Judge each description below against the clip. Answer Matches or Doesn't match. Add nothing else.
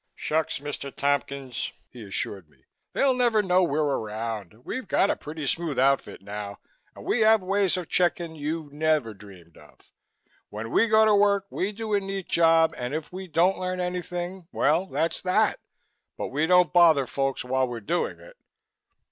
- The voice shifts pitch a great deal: Matches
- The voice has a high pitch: Doesn't match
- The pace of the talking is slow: Doesn't match